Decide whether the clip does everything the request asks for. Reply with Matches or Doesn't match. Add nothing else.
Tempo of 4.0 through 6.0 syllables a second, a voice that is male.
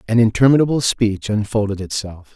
Matches